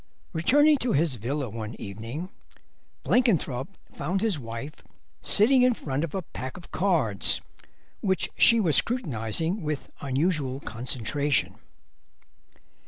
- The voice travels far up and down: Yes, wide, 7.0 semitones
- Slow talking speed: Yes, slow, 115 wpm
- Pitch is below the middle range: No, medium, 150 Hz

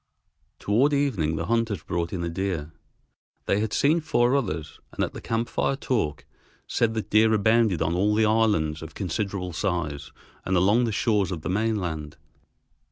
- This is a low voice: Yes, low, 100 Hz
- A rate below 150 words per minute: No, average, 170 wpm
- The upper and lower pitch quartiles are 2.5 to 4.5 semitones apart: No, average, 5.0 semitones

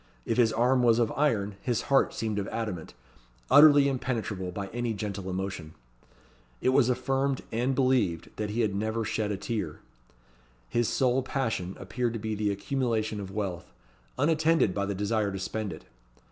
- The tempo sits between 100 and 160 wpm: No, average, 170 wpm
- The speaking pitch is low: Yes, low, 110 Hz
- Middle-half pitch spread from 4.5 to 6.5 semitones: No, average, 4.1 semitones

